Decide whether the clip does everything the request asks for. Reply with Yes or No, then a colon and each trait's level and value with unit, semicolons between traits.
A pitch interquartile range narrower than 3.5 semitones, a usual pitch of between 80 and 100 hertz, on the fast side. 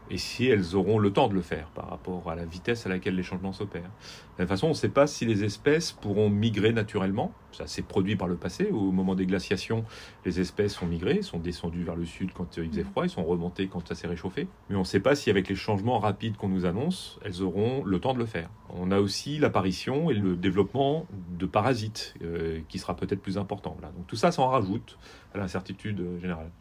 Yes: average, 3.0 semitones; very low, 95 Hz; fast, 240 wpm